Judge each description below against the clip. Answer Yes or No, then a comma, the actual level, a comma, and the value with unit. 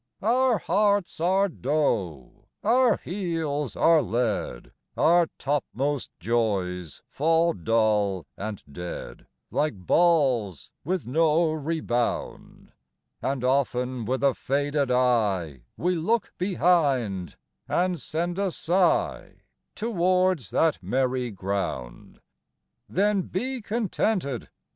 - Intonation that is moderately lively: No, wide, 7.8 semitones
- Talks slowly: Yes, slow, 100 wpm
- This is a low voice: No, medium, 145 Hz